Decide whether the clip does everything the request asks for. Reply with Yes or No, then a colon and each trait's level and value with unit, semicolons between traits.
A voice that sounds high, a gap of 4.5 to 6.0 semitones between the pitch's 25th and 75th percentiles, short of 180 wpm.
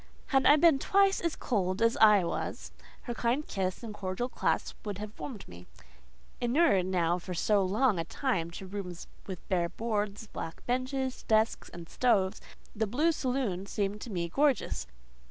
Yes: high, 210 Hz; wide, 5.4 semitones; average, 170 wpm